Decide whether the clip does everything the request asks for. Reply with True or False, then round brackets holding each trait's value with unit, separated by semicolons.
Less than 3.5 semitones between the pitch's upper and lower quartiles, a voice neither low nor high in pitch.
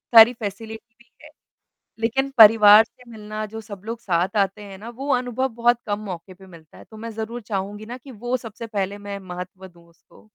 False (2.8 semitones; 215 Hz)